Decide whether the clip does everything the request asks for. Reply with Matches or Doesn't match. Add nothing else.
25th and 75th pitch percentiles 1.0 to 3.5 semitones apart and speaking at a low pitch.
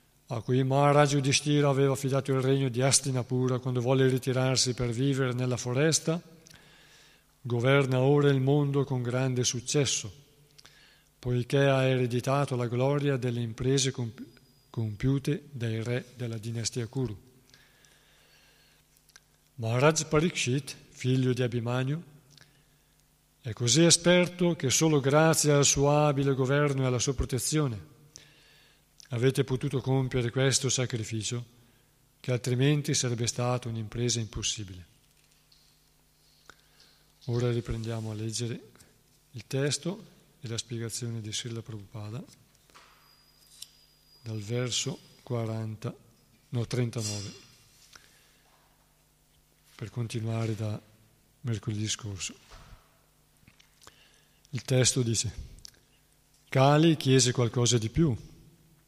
Matches